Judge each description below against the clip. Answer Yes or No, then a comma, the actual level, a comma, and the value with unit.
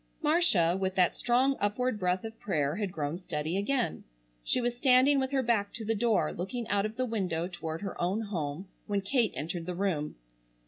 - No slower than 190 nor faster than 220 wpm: Yes, average, 195 wpm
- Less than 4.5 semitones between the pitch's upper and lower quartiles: No, wide, 5.5 semitones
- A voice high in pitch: Yes, high, 200 Hz